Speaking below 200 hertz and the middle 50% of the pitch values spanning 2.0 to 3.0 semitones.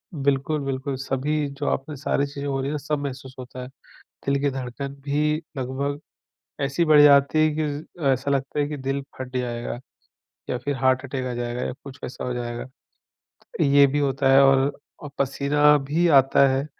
No: medium, 140 Hz; narrow, 1.6 semitones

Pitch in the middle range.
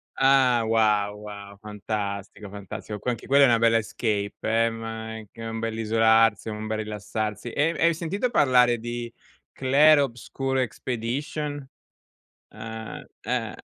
No: low, 115 Hz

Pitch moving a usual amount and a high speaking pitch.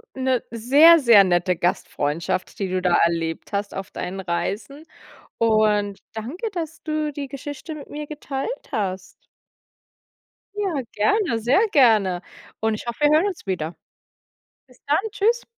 No: wide, 7.7 semitones; high, 230 Hz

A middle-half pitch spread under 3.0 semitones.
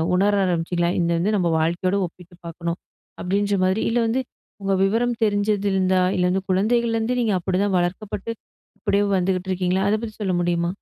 Yes: narrow, 2.6 semitones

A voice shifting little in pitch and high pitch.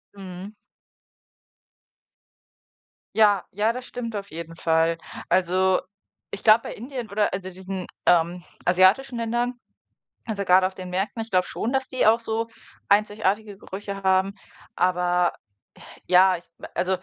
No: average, 3.2 semitones; high, 195 Hz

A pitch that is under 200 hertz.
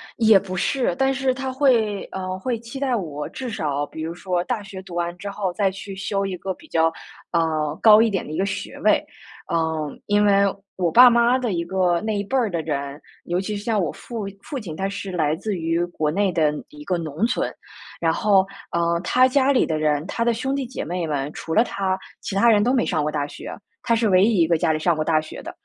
Yes: high, 190 Hz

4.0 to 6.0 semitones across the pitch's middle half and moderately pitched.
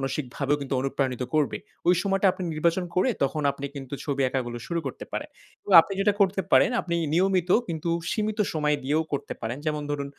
Yes: average, 4.8 semitones; medium, 150 Hz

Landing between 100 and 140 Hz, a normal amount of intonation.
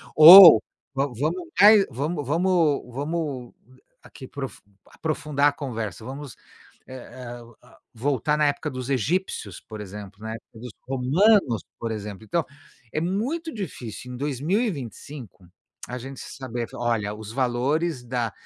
Yes: low, 135 Hz; average, 4.9 semitones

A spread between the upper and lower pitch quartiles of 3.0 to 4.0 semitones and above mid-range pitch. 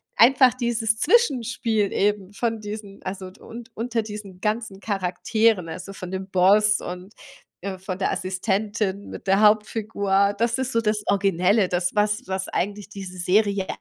No: narrow, 2.6 semitones; high, 205 Hz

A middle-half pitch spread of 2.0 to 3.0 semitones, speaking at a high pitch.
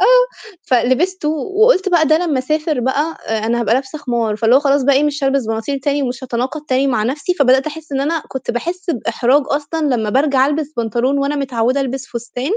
No: average, 3.6 semitones; very high, 275 Hz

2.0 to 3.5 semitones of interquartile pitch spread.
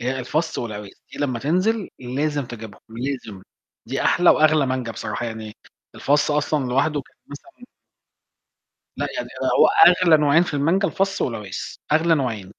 No: average, 4.9 semitones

